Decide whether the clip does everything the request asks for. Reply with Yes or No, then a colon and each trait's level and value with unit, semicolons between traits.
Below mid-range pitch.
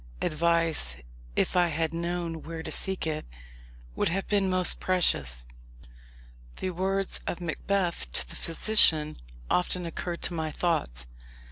No: medium, 170 Hz